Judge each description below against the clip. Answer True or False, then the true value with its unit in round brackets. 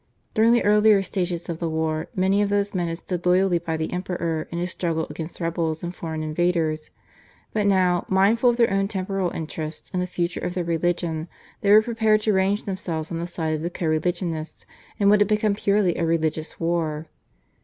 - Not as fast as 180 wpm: False (205 wpm)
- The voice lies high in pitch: False (175 Hz)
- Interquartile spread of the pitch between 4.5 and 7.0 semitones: False (3.4 semitones)